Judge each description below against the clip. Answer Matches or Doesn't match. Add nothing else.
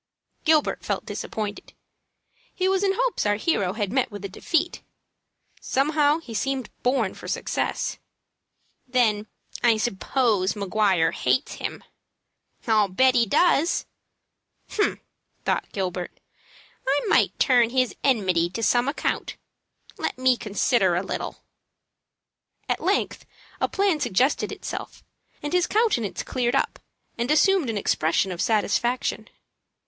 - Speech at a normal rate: Doesn't match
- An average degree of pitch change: Doesn't match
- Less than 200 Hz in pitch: Doesn't match